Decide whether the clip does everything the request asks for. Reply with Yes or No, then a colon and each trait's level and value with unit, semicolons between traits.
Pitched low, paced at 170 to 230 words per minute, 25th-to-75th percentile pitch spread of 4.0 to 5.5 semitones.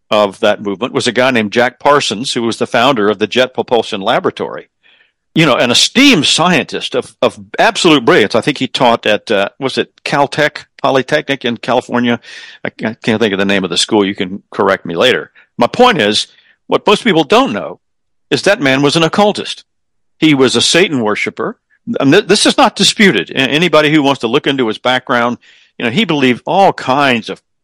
Yes: low, 130 Hz; average, 200 wpm; average, 4.3 semitones